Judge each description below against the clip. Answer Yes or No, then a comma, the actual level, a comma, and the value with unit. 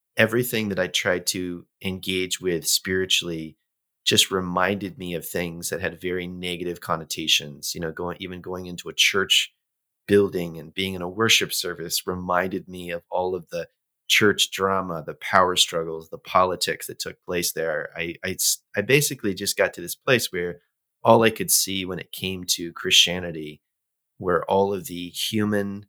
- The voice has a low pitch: Yes, very low, 90 Hz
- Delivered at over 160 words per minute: Yes, average, 170 wpm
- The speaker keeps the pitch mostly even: Yes, narrow, 1.7 semitones